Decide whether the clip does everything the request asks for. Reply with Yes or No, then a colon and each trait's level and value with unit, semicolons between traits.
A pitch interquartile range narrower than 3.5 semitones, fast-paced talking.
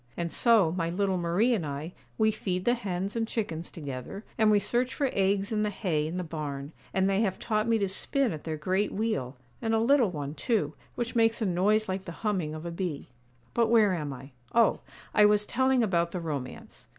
No: average, 5.0 semitones; fast, 220 wpm